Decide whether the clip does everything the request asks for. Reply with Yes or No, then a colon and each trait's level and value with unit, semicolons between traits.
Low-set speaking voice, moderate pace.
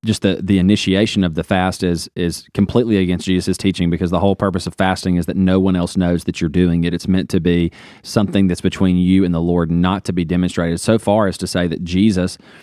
No: very low, 95 Hz; fast, 240 wpm